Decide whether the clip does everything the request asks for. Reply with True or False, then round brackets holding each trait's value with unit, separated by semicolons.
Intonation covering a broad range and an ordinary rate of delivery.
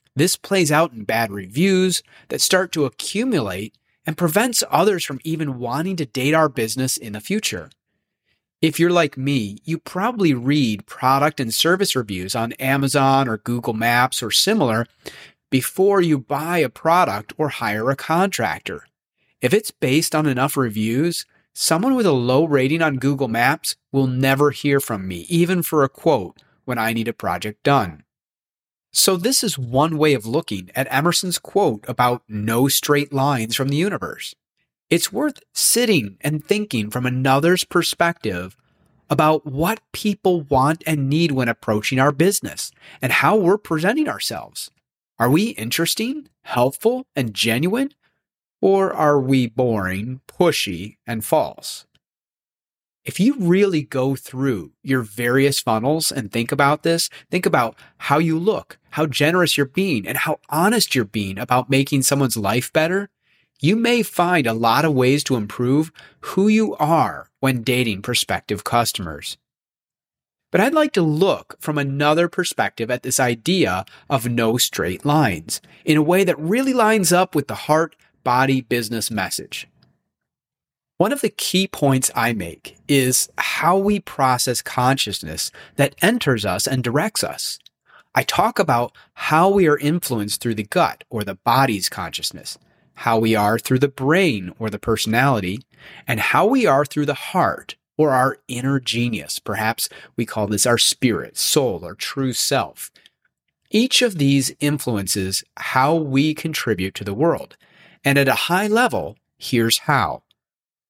True (5.9 semitones; 155 wpm)